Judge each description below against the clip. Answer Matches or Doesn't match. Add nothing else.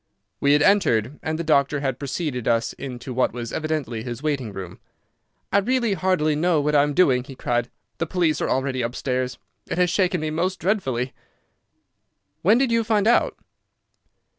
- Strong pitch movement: Matches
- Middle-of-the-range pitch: Matches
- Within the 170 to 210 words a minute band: Matches